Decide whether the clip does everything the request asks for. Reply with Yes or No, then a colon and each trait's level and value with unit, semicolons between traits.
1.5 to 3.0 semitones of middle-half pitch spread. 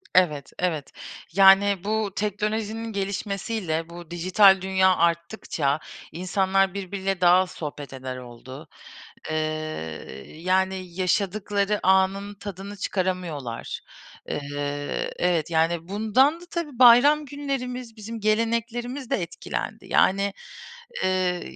No: average, 3.7 semitones